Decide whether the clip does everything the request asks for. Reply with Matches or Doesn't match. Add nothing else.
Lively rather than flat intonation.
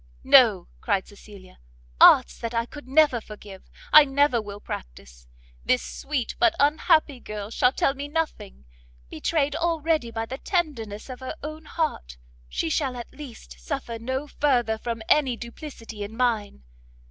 Matches